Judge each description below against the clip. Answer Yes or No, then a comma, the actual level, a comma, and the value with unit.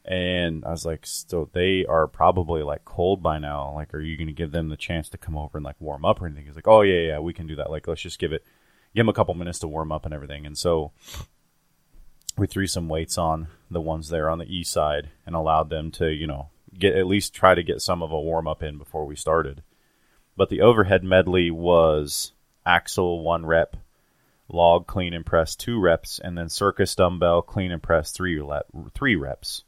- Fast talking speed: Yes, fast, 225 wpm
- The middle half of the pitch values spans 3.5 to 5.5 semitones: No, narrow, 2.4 semitones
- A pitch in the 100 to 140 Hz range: No, very low, 80 Hz